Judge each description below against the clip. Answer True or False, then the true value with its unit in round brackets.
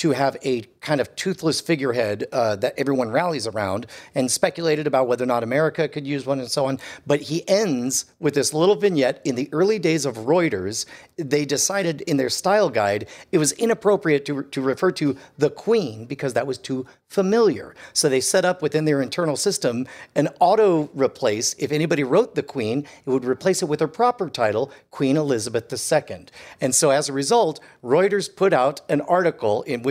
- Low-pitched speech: False (150 Hz)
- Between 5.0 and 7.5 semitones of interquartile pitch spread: False (4.6 semitones)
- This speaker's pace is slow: False (195 wpm)